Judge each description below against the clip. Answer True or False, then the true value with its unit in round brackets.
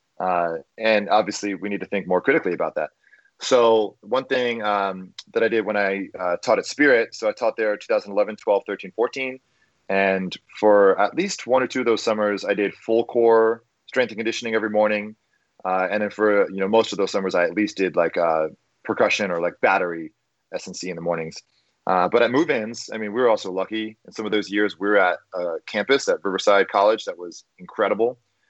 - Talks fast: True (215 wpm)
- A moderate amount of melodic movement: True (3.8 semitones)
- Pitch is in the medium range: False (105 Hz)